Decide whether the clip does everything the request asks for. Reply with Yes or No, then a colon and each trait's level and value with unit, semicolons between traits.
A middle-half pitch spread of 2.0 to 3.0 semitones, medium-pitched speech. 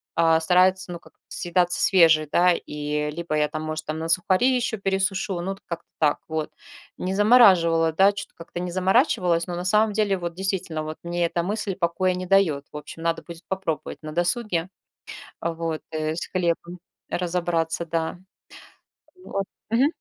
Yes: average, 2.7 semitones; medium, 175 Hz